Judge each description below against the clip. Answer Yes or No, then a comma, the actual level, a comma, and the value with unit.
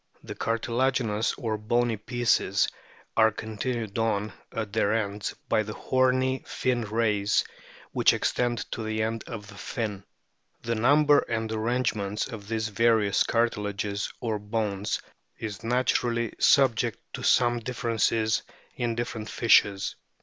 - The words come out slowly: Yes, slow, 130 wpm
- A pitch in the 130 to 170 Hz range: No, low, 115 Hz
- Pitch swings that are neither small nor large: No, narrow, 2.0 semitones